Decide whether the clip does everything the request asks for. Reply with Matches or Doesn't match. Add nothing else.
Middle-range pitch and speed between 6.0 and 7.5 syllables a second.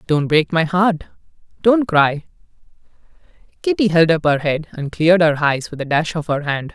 Doesn't match